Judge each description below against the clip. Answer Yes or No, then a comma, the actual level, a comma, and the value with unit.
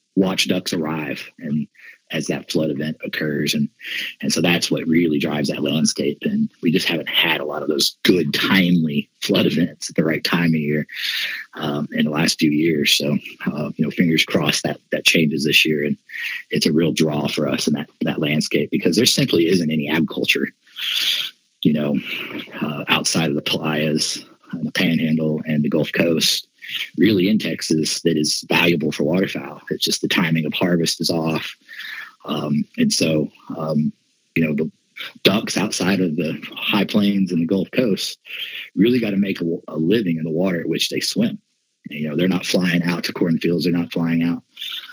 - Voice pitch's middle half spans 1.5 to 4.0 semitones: Yes, average, 2.8 semitones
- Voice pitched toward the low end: Yes, very low, 80 Hz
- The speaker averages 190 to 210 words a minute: Yes, average, 195 wpm